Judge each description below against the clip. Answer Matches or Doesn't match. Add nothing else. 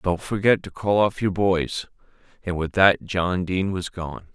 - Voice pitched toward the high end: Doesn't match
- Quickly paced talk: Doesn't match